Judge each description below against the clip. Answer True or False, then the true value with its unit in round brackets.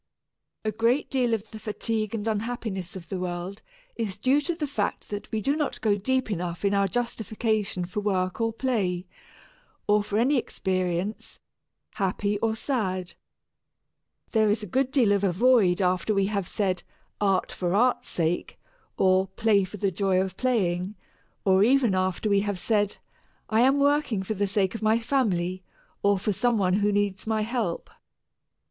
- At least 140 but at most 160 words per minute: False (175 wpm)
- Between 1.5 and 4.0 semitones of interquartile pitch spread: True (3.3 semitones)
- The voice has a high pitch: True (205 Hz)